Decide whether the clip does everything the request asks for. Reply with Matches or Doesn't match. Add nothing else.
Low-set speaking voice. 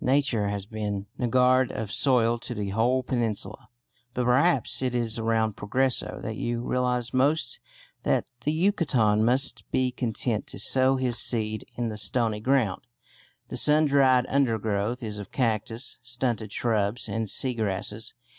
Matches